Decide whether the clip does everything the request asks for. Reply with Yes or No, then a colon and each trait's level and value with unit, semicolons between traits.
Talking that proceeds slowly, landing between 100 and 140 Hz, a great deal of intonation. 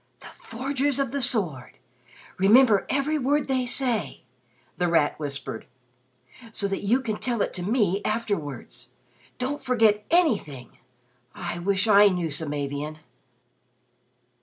No: slow, 125 wpm; high, 210 Hz; wide, 6.9 semitones